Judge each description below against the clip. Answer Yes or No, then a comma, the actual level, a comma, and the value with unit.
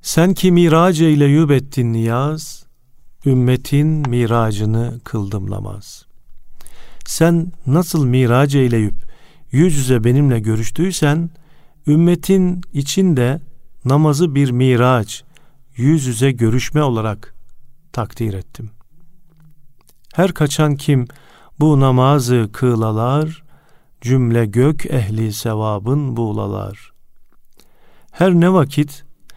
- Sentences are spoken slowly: Yes, slow, 85 wpm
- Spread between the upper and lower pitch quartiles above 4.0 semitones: Yes, average, 4.6 semitones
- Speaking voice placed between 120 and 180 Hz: Yes, low, 135 Hz